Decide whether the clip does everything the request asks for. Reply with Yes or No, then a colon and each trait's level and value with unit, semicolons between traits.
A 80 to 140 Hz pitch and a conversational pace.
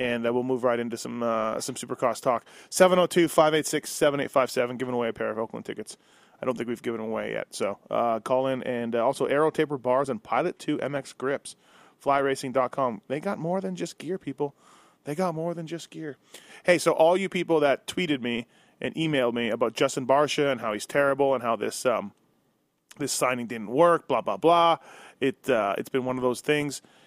No: low, 135 Hz; fast, 210 wpm